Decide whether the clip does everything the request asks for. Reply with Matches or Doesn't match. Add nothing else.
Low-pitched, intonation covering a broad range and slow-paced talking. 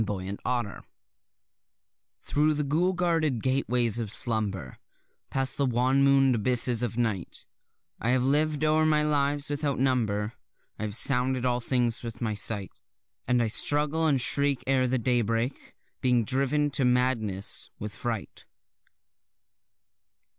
Doesn't match